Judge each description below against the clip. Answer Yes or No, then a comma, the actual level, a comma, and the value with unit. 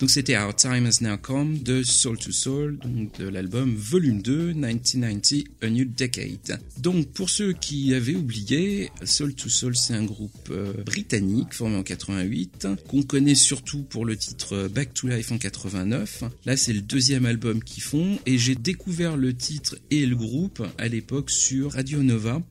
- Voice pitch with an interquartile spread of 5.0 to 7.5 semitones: No, average, 4.0 semitones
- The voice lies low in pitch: Yes, low, 130 Hz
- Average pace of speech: Yes, average, 180 wpm